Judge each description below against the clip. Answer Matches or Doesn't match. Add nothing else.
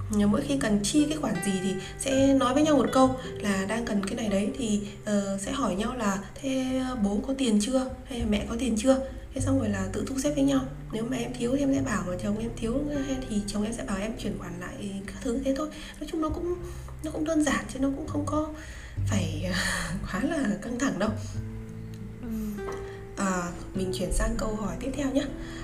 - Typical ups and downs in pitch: Doesn't match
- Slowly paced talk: Doesn't match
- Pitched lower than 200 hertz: Doesn't match